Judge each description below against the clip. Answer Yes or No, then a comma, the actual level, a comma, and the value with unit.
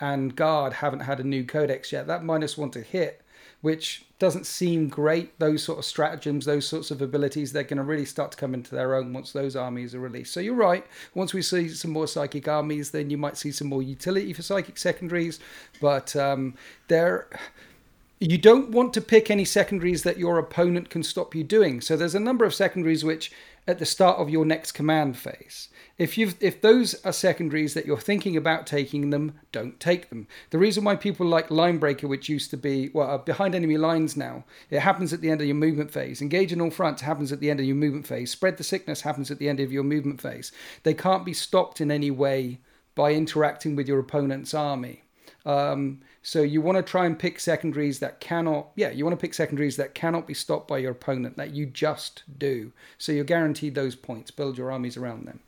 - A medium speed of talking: No, fast, 220 wpm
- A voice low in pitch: No, medium, 155 Hz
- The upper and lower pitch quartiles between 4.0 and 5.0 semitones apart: No, average, 3.2 semitones